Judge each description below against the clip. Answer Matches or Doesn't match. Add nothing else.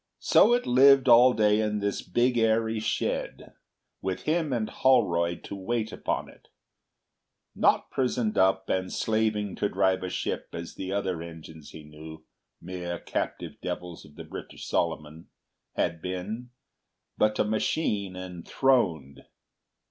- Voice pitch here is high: Doesn't match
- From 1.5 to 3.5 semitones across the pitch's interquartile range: Doesn't match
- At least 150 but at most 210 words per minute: Doesn't match